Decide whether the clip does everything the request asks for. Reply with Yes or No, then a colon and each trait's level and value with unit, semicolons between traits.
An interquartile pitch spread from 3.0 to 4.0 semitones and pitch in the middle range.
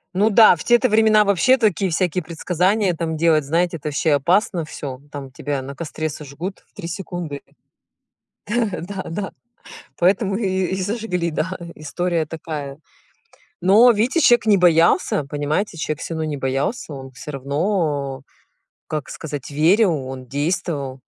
No: average, 4.9 semitones; medium, 170 Hz